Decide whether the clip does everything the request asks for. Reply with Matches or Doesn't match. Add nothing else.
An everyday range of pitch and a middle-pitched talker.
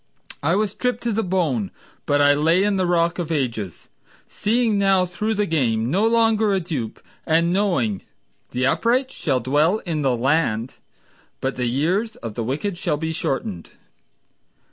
Doesn't match